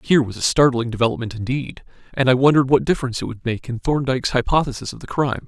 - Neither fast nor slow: No, fast, 220 wpm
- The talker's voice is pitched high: No, low, 130 Hz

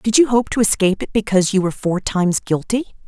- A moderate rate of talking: No, fast, 235 wpm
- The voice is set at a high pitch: Yes, high, 205 Hz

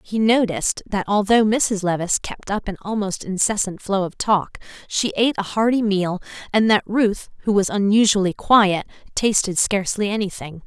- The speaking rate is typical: Yes, average, 165 wpm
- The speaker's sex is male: No, female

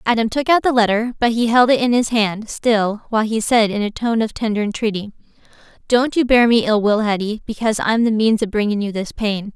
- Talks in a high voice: Yes, high, 220 Hz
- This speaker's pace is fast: Yes, fast, 240 wpm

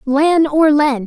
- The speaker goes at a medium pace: Yes, average, 170 wpm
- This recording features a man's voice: No, female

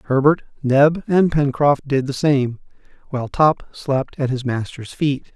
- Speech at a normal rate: Yes, average, 155 wpm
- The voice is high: No, medium, 140 Hz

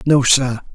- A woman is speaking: No, male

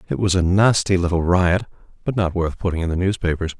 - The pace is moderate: No, fast, 215 wpm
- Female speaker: No, male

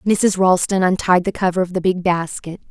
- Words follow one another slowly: No, average, 200 wpm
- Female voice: Yes, female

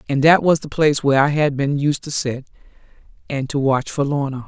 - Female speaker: Yes, female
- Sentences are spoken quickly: Yes, fast, 230 wpm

